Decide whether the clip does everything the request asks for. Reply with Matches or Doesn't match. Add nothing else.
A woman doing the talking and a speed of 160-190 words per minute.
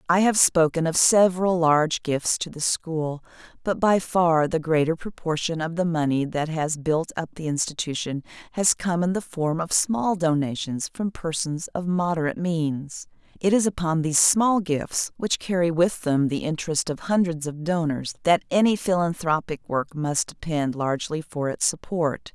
Matches